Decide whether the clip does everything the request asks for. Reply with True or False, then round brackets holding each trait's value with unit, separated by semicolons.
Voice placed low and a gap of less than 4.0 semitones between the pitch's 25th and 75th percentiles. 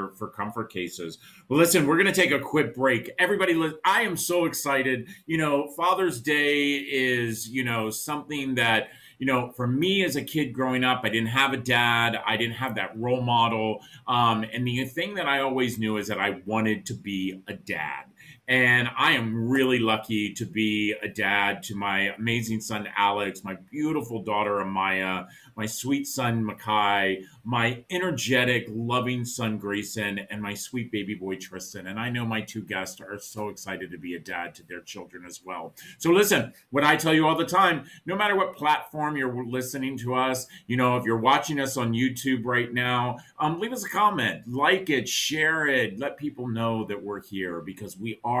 False (120 Hz; 4.6 semitones)